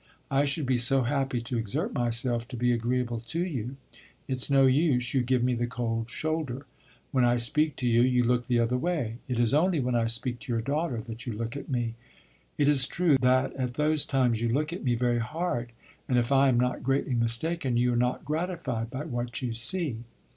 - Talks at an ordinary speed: No, fast, 220 wpm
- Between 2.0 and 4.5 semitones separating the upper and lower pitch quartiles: Yes, average, 2.8 semitones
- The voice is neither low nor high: No, low, 125 Hz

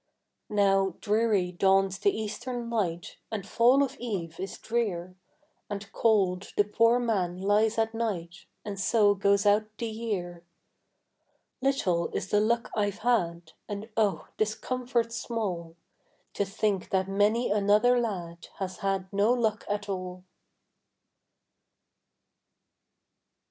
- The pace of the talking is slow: Yes, slow, 125 wpm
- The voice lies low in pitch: No, high, 205 Hz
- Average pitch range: Yes, average, 3.1 semitones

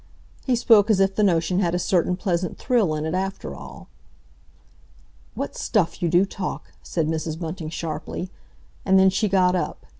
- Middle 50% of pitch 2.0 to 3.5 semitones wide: Yes, average, 2.7 semitones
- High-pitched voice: No, medium, 180 Hz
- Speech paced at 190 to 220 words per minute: No, average, 175 wpm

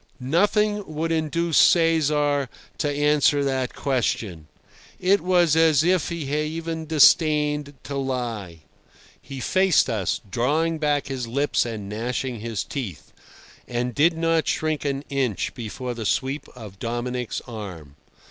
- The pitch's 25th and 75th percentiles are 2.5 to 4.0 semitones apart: No, average, 4.8 semitones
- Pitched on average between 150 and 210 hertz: No, medium, 140 Hz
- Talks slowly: Yes, slow, 130 wpm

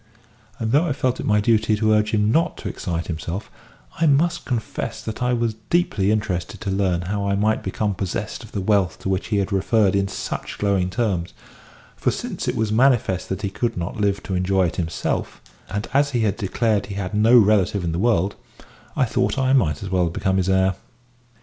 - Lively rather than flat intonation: No, average, 3.1 semitones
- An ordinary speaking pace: No, fast, 215 wpm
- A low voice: Yes, low, 105 Hz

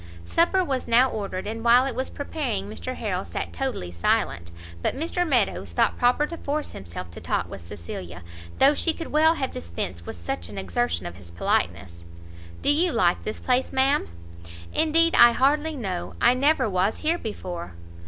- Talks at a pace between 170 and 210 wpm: Yes, average, 180 wpm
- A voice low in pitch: No, high, 230 Hz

